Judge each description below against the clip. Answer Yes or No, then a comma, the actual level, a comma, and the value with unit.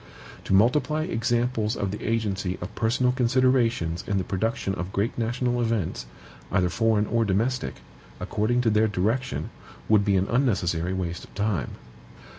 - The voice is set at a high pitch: No, low, 110 Hz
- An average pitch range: Yes, average, 4.0 semitones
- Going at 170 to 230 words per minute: No, average, 150 wpm